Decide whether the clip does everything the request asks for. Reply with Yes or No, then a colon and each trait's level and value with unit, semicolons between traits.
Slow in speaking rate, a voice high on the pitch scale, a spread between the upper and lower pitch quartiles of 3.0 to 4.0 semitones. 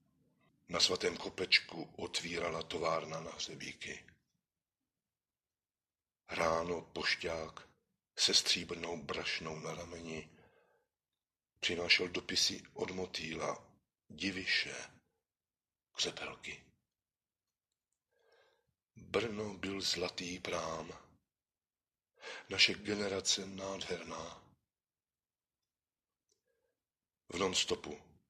No: slow, 65 wpm; very low, 90 Hz; average, 3.4 semitones